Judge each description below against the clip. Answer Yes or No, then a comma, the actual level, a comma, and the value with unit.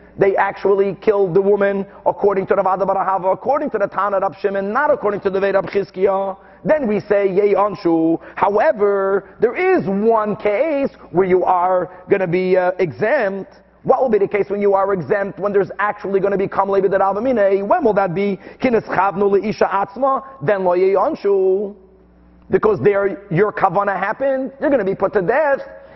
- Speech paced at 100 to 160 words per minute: No, average, 185 wpm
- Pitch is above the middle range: Yes, high, 200 Hz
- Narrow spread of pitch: Yes, narrow, 1.3 semitones